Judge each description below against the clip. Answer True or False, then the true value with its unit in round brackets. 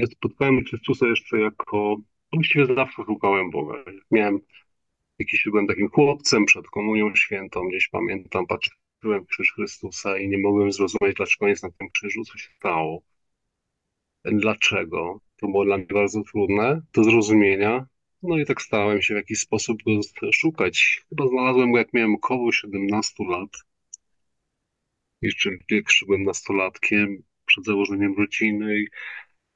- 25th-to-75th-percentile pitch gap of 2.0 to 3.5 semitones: True (2.7 semitones)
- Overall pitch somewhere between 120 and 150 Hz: False (105 Hz)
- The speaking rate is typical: True (140 wpm)